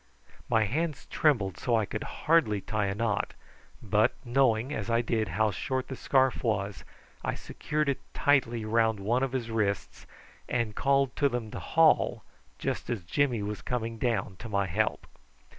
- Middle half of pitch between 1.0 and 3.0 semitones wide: No, average, 3.8 semitones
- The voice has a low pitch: Yes, low, 115 Hz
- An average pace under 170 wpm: No, average, 175 wpm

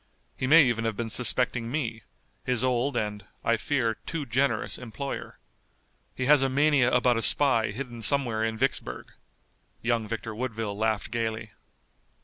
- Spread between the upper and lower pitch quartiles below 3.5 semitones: Yes, average, 2.8 semitones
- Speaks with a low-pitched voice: Yes, low, 120 Hz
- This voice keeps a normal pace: Yes, average, 150 wpm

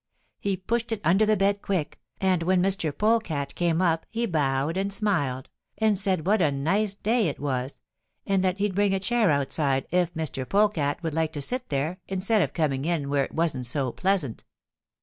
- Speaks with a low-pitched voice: No, medium, 180 Hz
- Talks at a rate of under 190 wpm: No, average, 195 wpm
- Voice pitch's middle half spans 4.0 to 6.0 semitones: Yes, wide, 5.5 semitones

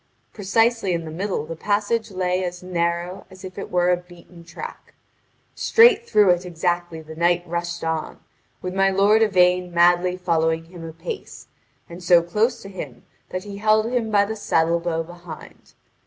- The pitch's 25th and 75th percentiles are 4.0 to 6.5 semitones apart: No, average, 2.7 semitones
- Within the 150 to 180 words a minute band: Yes, average, 170 wpm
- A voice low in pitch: No, medium, 180 Hz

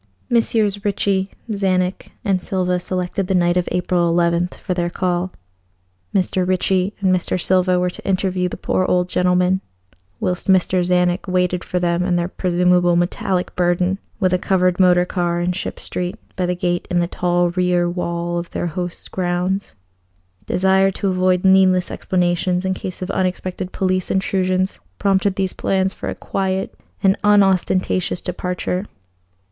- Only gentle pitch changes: Yes, narrow, 1.1 semitones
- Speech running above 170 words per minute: No, average, 155 wpm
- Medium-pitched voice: Yes, medium, 180 Hz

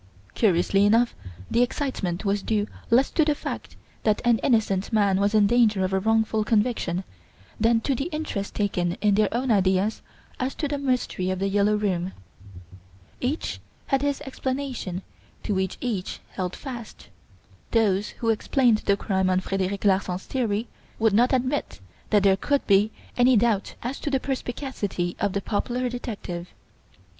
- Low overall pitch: No, high, 215 Hz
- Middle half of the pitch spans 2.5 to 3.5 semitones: No, average, 4.2 semitones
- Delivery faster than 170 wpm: No, average, 160 wpm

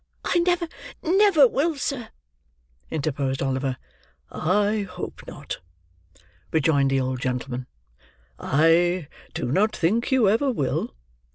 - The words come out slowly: Yes, slow, 110 wpm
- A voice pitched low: No, medium, 175 Hz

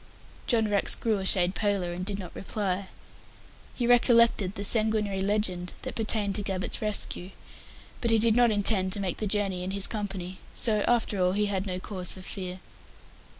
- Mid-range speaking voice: No, high, 200 Hz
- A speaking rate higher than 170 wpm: Yes, average, 185 wpm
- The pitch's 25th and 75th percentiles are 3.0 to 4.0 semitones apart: No, narrow, 2.5 semitones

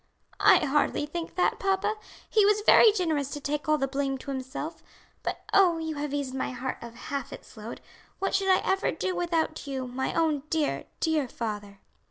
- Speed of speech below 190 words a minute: No, average, 195 wpm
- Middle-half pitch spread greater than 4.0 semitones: Yes, average, 4.6 semitones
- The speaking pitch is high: Yes, very high, 295 Hz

